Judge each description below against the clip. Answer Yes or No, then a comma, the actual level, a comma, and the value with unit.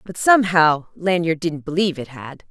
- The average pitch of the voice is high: No, medium, 170 Hz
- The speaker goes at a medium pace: Yes, average, 170 wpm